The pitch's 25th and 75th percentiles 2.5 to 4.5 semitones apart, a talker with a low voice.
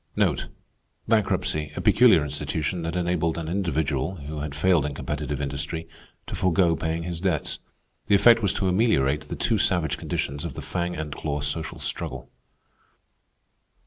Yes: average, 3.5 semitones; very low, 80 Hz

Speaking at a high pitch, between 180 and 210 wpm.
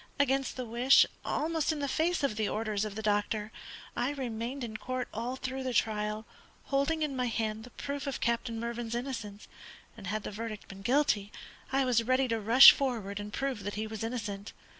Yes: high, 235 Hz; average, 200 wpm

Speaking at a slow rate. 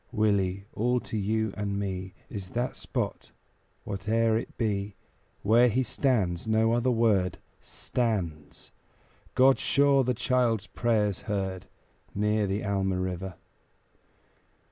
Yes: slow, 120 wpm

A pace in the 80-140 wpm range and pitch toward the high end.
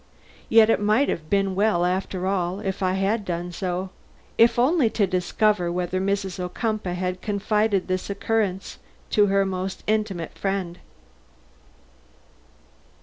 Yes: slow, 135 wpm; high, 195 Hz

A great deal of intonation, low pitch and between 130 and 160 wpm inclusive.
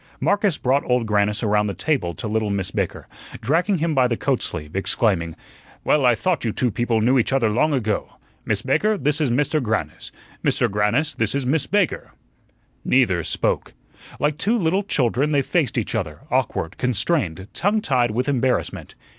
No: wide, 5.9 semitones; low, 125 Hz; average, 180 wpm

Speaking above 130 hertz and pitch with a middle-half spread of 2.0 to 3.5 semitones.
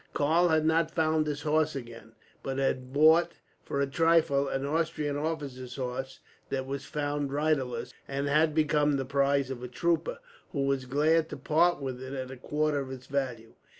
Yes: medium, 140 Hz; average, 2.8 semitones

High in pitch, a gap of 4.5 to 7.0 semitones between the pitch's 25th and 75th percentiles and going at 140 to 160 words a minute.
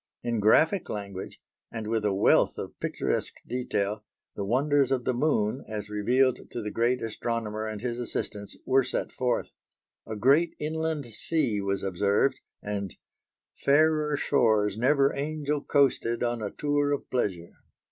No: low, 120 Hz; average, 5.1 semitones; average, 145 wpm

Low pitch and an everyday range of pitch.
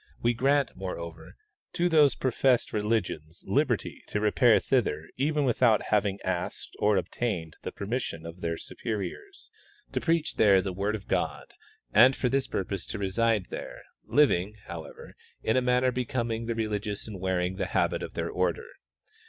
Yes: low, 110 Hz; average, 5.0 semitones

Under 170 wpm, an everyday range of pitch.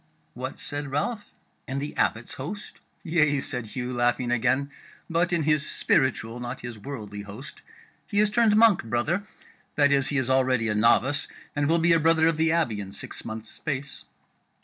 No: average, 180 wpm; average, 5.0 semitones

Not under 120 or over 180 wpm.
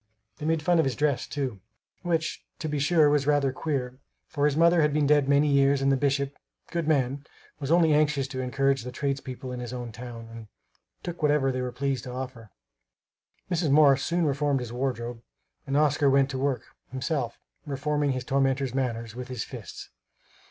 No: average, 190 wpm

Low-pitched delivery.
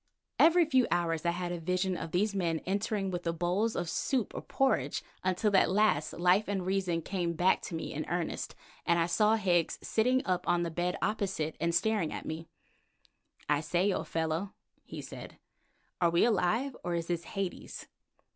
No: medium, 180 Hz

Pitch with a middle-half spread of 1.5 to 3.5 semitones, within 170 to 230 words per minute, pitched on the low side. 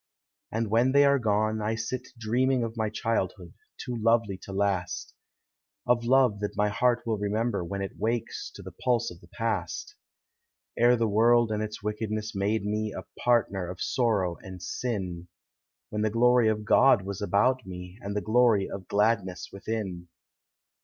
Yes: average, 2.9 semitones; average, 180 wpm; low, 110 Hz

